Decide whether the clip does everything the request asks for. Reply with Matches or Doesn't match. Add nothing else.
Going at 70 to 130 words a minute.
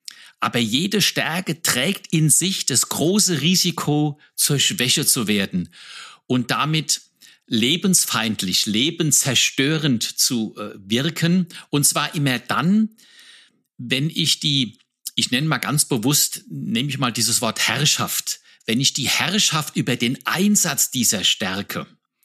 Matches